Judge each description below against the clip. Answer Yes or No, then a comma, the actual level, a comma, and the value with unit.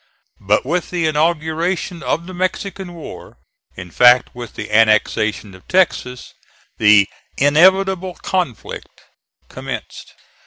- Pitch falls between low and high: Yes, medium, 160 Hz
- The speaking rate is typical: No, slow, 110 wpm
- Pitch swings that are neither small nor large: No, wide, 8.1 semitones